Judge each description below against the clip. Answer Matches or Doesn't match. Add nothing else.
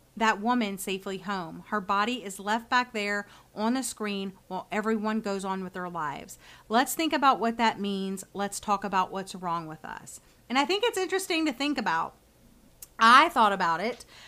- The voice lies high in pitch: Matches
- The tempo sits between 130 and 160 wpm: Doesn't match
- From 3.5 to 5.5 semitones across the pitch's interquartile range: Matches